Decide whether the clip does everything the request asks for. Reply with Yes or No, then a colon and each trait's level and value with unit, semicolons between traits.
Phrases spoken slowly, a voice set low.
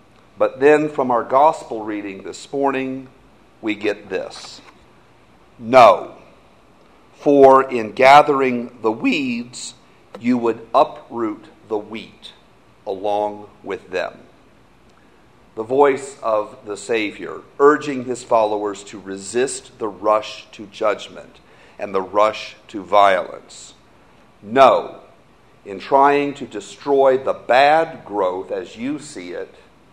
Yes: slow, 110 wpm; low, 125 Hz